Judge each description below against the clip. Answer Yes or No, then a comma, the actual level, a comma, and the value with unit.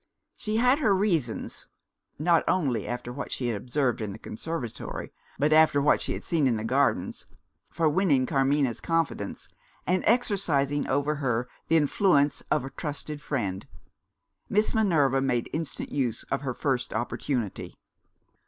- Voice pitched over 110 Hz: Yes, medium, 140 Hz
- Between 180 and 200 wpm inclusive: No, average, 150 wpm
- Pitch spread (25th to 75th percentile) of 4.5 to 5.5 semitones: Yes, average, 4.8 semitones